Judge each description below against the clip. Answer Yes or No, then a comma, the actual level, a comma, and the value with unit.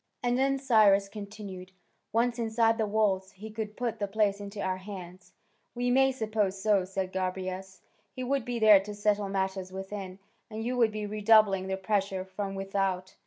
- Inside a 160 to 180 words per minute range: Yes, average, 175 wpm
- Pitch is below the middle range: No, high, 205 Hz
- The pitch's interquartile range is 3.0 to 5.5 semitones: No, narrow, 2.5 semitones